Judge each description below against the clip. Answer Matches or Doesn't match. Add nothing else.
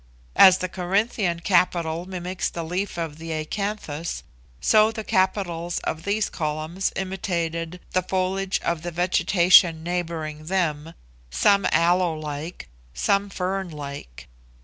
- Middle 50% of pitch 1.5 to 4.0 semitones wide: Matches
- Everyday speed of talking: Doesn't match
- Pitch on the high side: Doesn't match